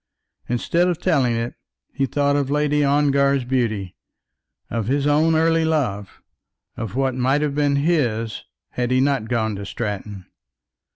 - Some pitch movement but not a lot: Yes, average, 4.1 semitones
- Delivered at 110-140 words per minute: No, average, 150 wpm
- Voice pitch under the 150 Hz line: Yes, low, 135 Hz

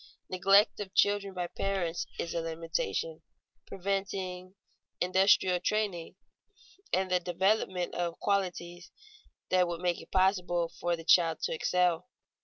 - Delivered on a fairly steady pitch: Yes, narrow, 2.0 semitones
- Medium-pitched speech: Yes, medium, 180 Hz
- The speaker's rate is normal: No, slow, 125 wpm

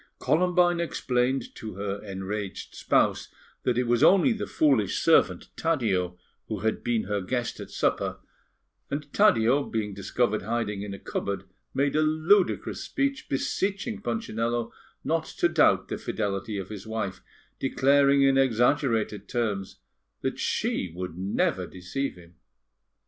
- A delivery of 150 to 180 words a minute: No, average, 140 wpm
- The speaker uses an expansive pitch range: Yes, wide, 5.9 semitones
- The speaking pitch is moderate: No, low, 120 Hz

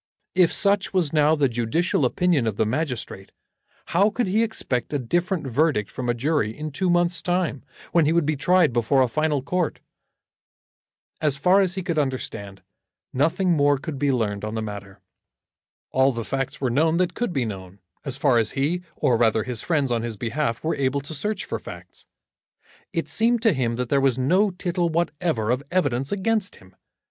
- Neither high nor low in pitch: Yes, medium, 145 Hz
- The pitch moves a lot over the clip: Yes, wide, 6.4 semitones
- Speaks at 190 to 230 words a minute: Yes, average, 195 wpm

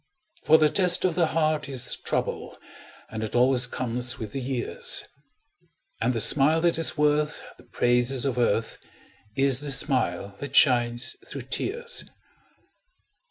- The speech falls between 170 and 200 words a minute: No, average, 145 wpm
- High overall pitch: No, low, 135 Hz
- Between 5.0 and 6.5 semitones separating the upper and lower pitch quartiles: No, average, 3.7 semitones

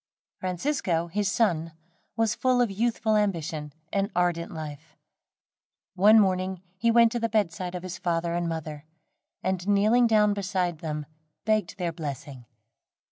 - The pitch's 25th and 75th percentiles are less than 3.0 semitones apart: No, average, 4.2 semitones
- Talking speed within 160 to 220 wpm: No, average, 140 wpm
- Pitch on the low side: No, medium, 185 Hz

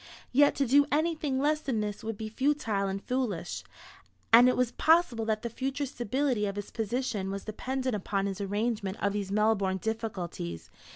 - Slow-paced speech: No, average, 175 wpm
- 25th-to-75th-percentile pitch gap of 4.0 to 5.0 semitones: Yes, average, 4.7 semitones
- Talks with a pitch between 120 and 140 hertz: No, high, 225 Hz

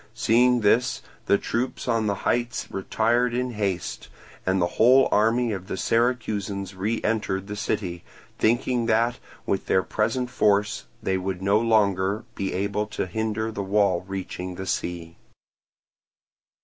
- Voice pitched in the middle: No, low, 105 Hz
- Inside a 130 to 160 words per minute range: Yes, average, 145 wpm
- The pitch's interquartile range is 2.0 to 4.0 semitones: Yes, average, 3.3 semitones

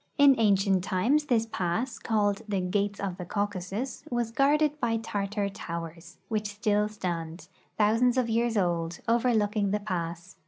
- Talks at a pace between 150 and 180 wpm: Yes, average, 155 wpm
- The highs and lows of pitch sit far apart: No, average, 3.7 semitones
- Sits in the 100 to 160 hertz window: No, high, 205 Hz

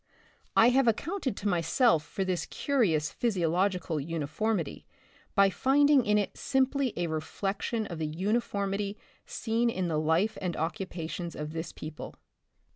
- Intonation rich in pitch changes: Yes, wide, 5.7 semitones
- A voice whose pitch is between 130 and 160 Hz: No, high, 195 Hz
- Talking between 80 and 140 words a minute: Yes, slow, 135 wpm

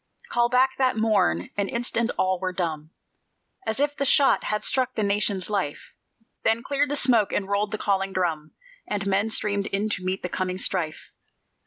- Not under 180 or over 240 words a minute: Yes, average, 185 wpm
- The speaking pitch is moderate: No, high, 205 Hz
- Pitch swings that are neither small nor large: Yes, average, 4.0 semitones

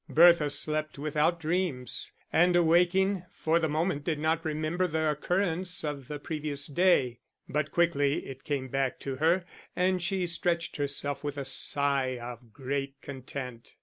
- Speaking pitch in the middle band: Yes, medium, 155 Hz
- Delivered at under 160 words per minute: Yes, average, 150 wpm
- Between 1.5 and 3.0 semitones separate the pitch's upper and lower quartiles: No, average, 3.6 semitones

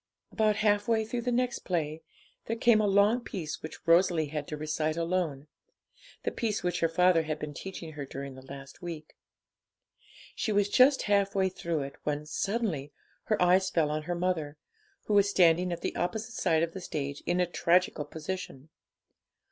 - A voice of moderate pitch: Yes, medium, 175 Hz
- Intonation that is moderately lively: Yes, average, 4.8 semitones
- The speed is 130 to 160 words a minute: No, average, 185 wpm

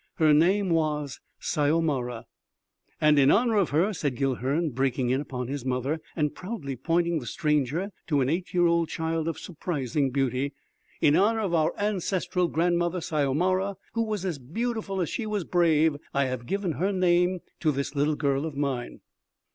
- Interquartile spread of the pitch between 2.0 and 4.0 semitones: No, average, 4.5 semitones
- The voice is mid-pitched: Yes, medium, 160 Hz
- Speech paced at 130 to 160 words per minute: No, average, 170 wpm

